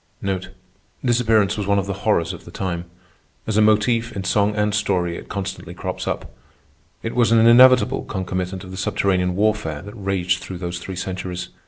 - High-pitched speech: No, low, 100 Hz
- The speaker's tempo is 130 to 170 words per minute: No, average, 180 wpm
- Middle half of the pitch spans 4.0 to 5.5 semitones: No, average, 2.8 semitones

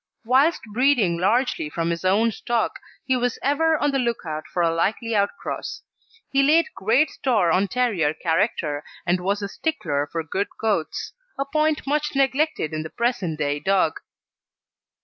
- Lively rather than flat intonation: Yes, wide, 8.2 semitones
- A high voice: Yes, high, 215 Hz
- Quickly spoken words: No, average, 165 wpm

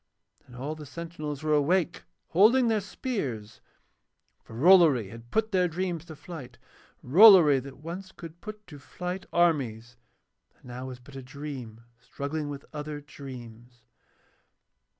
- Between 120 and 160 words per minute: Yes, average, 140 wpm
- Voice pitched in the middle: Yes, medium, 150 Hz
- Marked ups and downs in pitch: Yes, wide, 5.8 semitones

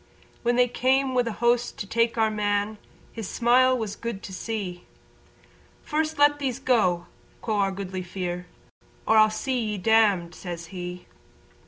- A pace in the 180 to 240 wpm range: No, average, 160 wpm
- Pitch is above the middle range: Yes, high, 220 Hz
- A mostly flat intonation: No, average, 4.2 semitones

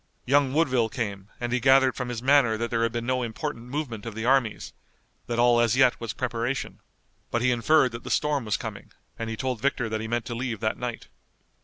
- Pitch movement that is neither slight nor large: No, narrow, 2.3 semitones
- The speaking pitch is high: No, low, 120 Hz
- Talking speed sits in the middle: No, fast, 225 wpm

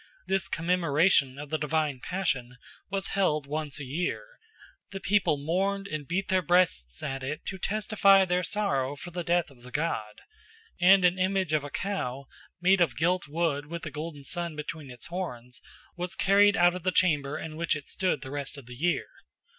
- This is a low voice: No, medium, 165 Hz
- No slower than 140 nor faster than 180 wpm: No, average, 190 wpm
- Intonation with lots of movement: No, average, 4.5 semitones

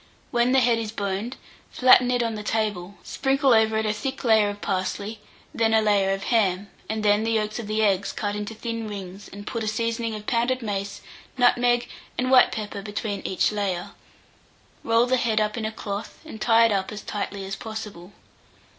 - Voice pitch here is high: Yes, high, 215 Hz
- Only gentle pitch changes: Yes, narrow, 2.2 semitones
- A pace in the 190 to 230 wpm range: Yes, average, 200 wpm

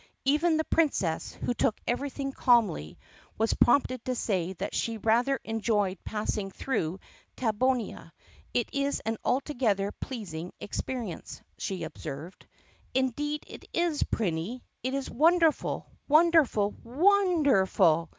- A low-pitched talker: No, high, 240 Hz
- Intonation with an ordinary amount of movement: No, wide, 6.0 semitones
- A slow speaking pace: Yes, slow, 120 wpm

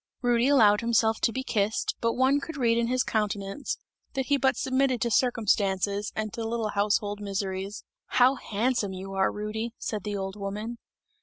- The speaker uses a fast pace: No, average, 175 wpm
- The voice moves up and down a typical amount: Yes, average, 3.2 semitones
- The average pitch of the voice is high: Yes, high, 220 Hz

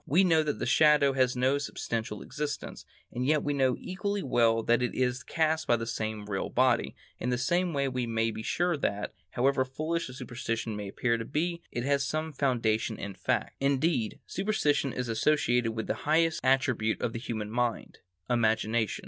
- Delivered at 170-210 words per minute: Yes, average, 180 wpm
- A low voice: Yes, low, 125 Hz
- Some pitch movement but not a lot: Yes, average, 4.6 semitones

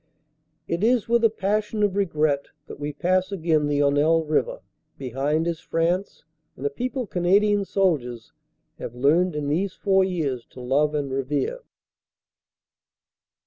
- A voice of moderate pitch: Yes, medium, 165 Hz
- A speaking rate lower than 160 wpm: Yes, average, 145 wpm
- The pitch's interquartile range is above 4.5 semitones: Yes, wide, 5.4 semitones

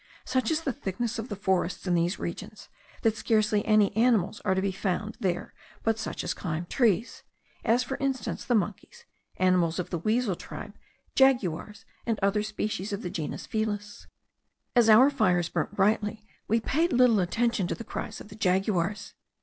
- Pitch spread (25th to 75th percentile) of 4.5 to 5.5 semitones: No, average, 3.5 semitones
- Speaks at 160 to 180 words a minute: Yes, average, 175 wpm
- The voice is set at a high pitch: Yes, high, 210 Hz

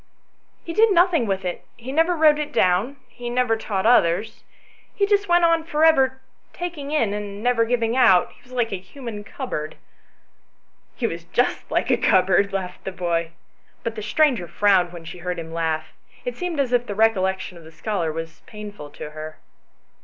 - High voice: Yes, high, 215 Hz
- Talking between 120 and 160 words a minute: No, average, 200 wpm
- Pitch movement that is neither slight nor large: No, wide, 7.4 semitones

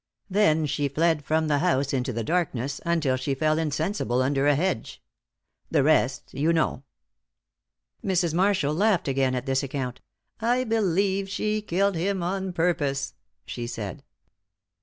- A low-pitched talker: No, medium, 160 Hz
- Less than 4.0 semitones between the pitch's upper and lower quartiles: No, wide, 5.5 semitones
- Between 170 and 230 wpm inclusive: No, average, 145 wpm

